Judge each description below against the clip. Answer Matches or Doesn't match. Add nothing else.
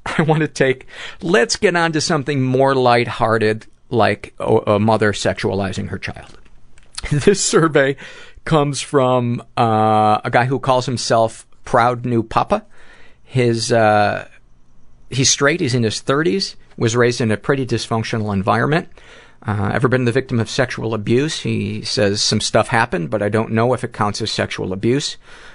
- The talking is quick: Doesn't match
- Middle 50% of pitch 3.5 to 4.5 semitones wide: Matches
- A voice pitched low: Matches